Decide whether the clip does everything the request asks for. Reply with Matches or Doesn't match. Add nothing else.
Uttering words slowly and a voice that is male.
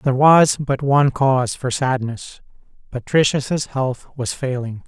Matches